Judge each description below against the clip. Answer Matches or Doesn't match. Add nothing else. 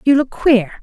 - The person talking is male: Doesn't match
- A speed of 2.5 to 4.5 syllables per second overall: Matches